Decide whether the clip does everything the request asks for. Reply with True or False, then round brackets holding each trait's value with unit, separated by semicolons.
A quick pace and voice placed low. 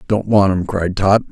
True (230 wpm; 100 Hz)